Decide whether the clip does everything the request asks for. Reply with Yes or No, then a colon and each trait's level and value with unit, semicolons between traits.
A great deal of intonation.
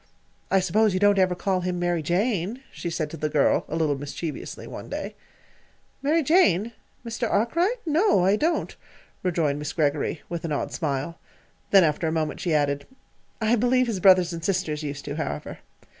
Yes: wide, 5.7 semitones